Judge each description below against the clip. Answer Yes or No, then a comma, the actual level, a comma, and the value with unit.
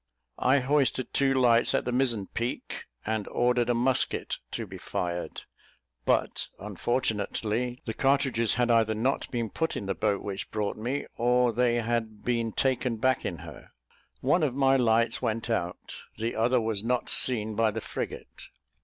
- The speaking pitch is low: Yes, low, 120 Hz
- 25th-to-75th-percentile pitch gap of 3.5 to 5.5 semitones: No, narrow, 2.4 semitones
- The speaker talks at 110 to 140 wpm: No, average, 165 wpm